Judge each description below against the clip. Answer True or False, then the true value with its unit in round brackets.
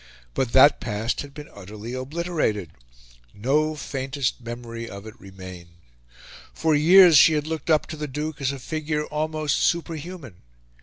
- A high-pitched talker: False (145 Hz)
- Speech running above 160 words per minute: False (150 wpm)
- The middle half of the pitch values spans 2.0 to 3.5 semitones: False (5.1 semitones)